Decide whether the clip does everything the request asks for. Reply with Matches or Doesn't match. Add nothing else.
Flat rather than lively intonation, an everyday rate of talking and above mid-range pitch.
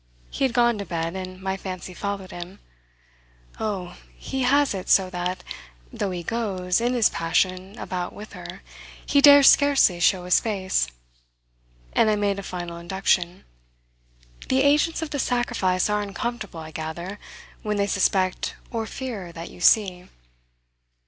Doesn't match